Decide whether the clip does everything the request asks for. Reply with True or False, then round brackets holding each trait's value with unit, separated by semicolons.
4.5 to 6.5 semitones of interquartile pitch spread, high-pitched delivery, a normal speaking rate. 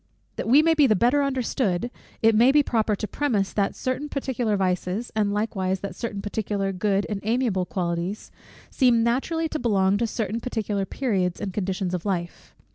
False (4.1 semitones; 215 Hz; 180 wpm)